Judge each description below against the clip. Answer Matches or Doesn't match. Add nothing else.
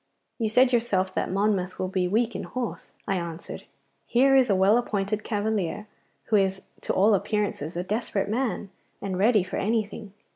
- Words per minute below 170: Doesn't match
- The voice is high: Matches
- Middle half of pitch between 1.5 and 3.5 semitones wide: Matches